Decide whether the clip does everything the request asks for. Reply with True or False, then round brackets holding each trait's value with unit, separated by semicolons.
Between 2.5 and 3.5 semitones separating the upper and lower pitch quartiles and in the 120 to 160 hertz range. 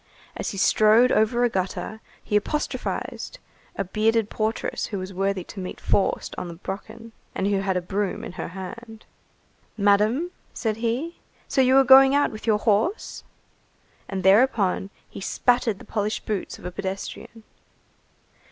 False (3.2 semitones; 215 Hz)